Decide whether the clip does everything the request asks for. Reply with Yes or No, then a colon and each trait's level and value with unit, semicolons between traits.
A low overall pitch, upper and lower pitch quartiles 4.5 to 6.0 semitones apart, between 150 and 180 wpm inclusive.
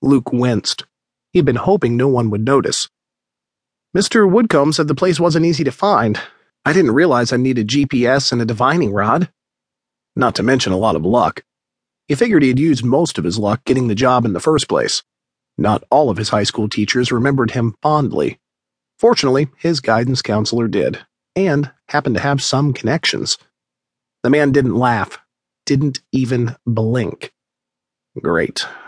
Yes: low, 125 Hz; average, 5.0 semitones; average, 165 wpm